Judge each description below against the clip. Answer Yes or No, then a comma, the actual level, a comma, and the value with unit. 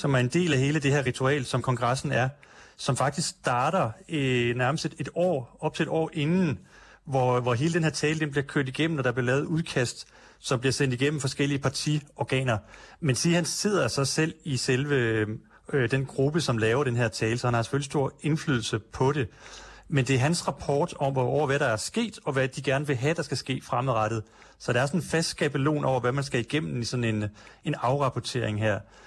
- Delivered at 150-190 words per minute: No, fast, 225 wpm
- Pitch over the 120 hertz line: Yes, low, 135 Hz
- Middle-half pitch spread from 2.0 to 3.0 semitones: No, average, 3.4 semitones